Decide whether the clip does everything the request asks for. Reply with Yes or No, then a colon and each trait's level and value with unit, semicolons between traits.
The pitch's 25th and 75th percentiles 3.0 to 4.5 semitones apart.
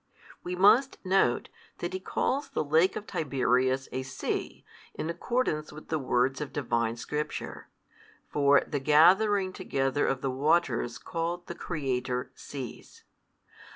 No: average, 5.1 semitones